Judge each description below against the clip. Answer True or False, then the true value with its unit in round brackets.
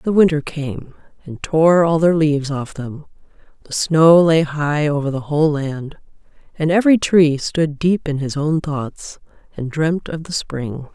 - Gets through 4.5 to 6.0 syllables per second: False (4.2 syllables/s)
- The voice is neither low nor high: True (155 Hz)